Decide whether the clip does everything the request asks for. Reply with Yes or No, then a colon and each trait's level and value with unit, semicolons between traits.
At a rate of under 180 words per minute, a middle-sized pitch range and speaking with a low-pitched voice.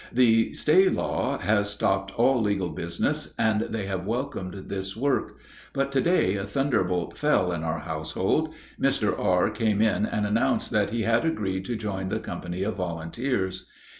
Yes: average, 165 wpm; average, 3.9 semitones; low, 105 Hz